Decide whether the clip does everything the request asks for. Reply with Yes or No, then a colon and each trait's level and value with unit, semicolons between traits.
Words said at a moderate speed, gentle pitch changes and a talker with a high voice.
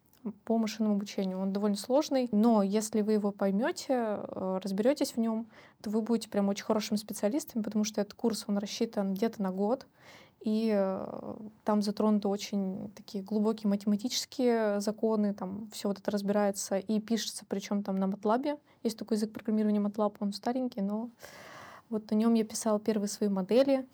No: fast, 165 wpm; narrow, 1.9 semitones; high, 215 Hz